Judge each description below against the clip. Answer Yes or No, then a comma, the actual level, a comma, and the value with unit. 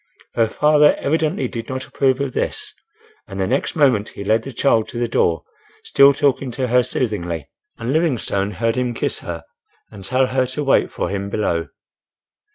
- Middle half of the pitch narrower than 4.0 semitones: No, average, 4.7 semitones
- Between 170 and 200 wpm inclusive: Yes, average, 180 wpm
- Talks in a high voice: No, low, 125 Hz